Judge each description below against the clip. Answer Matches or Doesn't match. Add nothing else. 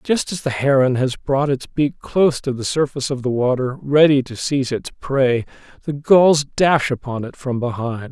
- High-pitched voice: Doesn't match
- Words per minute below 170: Doesn't match